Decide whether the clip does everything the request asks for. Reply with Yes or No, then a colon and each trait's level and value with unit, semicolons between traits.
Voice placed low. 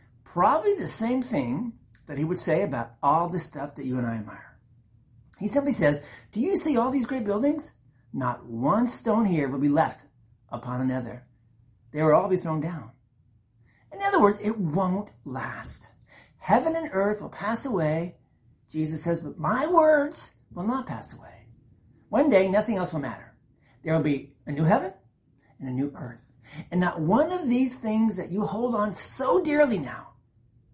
No: medium, 160 Hz